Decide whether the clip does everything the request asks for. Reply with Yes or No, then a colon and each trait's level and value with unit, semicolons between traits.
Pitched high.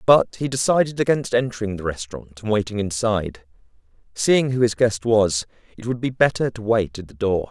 No: low, 110 Hz